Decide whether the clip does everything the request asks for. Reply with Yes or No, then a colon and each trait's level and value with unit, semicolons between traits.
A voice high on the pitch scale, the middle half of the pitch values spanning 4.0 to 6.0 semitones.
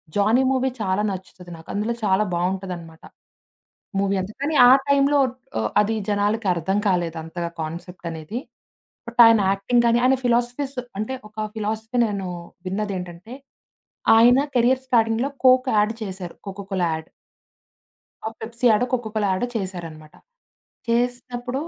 Yes: high, 210 Hz; average, 4.6 semitones